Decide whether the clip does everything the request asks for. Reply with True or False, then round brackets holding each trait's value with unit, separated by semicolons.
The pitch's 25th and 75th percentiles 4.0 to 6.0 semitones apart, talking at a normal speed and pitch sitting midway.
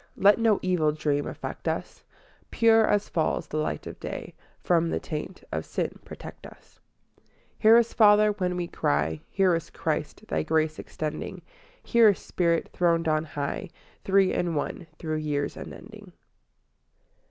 True (4.8 semitones; 155 wpm; 170 Hz)